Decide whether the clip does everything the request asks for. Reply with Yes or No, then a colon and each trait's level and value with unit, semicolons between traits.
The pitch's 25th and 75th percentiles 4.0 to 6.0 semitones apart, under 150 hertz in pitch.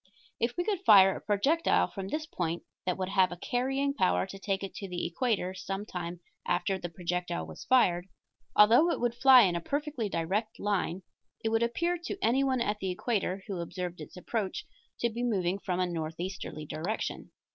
No: average, 5.1 semitones; high, 195 Hz